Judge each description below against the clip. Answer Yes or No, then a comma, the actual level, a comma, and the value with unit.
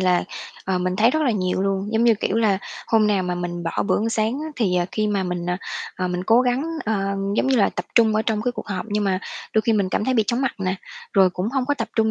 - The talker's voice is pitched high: Yes, high, 210 Hz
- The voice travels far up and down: No, average, 3.6 semitones